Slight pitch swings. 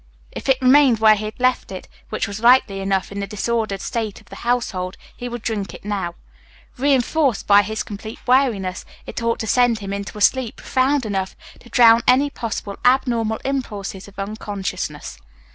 No: average, 3.7 semitones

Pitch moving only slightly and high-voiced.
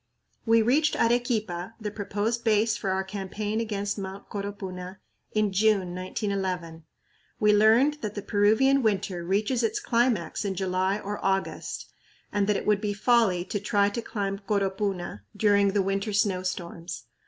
Yes: narrow, 2.3 semitones; high, 205 Hz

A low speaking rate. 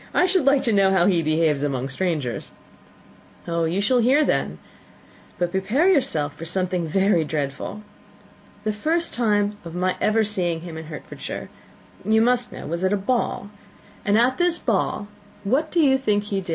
No: average, 170 wpm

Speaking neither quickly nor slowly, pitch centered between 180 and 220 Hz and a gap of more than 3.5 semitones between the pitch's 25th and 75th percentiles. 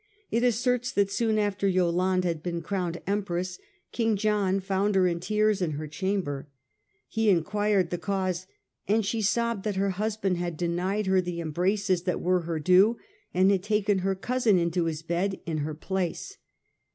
No: average, 175 wpm; high, 190 Hz; average, 3.0 semitones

